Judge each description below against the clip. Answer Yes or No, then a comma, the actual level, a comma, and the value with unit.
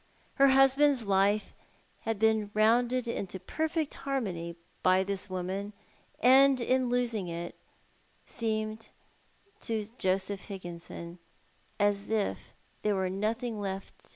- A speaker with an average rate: No, slow, 115 wpm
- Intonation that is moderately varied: Yes, average, 4.2 semitones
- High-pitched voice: Yes, high, 215 Hz